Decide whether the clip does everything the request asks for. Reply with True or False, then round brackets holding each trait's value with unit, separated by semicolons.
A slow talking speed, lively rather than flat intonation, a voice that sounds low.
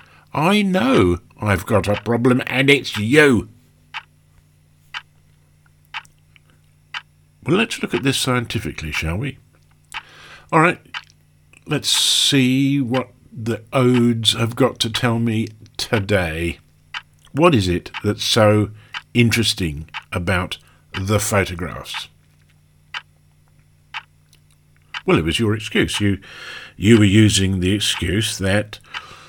True (105 wpm; 7.2 semitones; 105 Hz)